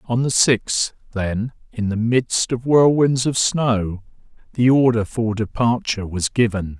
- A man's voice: Yes, male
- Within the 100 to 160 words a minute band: Yes, average, 150 wpm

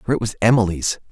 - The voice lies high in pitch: No, low, 105 Hz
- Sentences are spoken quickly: Yes, fast, 215 wpm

